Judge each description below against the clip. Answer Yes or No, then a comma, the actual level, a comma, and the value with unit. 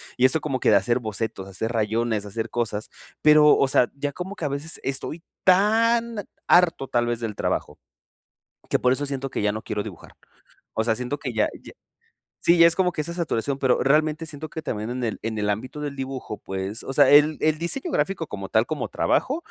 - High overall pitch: No, low, 135 Hz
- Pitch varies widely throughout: Yes, wide, 5.9 semitones